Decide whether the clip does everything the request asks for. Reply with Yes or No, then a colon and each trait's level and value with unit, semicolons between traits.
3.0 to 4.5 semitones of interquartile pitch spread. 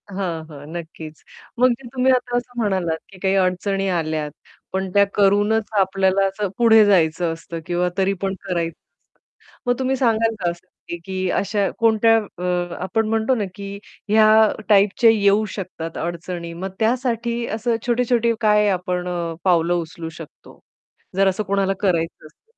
Yes: average, 4.1 semitones